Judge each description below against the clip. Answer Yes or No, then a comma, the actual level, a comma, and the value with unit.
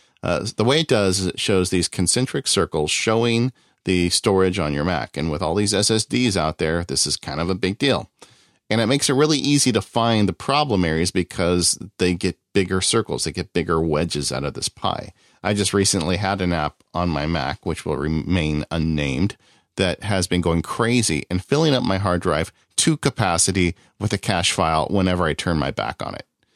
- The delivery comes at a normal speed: No, fast, 210 wpm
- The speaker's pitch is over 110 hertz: No, very low, 95 Hz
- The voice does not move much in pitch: No, average, 4.2 semitones